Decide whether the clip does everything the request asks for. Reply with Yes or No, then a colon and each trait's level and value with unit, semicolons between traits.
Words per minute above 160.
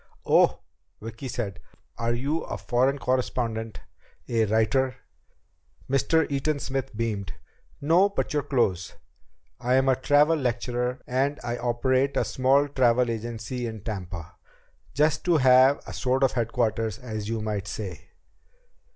No: slow, 135 wpm